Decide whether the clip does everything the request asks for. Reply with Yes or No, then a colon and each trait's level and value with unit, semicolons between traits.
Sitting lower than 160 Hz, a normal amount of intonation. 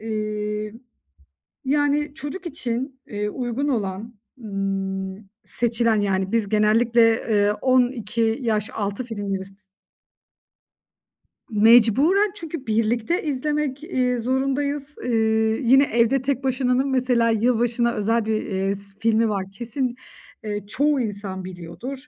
No: high, 230 Hz; average, 3.8 semitones